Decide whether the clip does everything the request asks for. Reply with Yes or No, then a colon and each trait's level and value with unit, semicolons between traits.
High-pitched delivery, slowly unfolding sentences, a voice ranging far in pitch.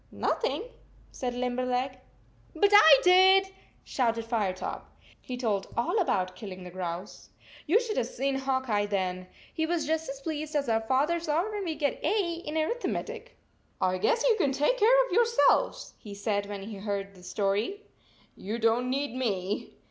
No: very high, 260 Hz; average, 185 wpm; wide, 8.5 semitones